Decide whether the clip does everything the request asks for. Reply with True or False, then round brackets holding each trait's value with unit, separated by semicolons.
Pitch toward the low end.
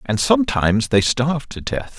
True (130 Hz)